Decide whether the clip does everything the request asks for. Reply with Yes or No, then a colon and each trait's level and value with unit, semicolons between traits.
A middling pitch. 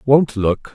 No: low, 120 Hz